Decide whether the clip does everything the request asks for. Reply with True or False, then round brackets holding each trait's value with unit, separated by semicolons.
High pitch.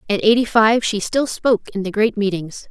True (210 Hz)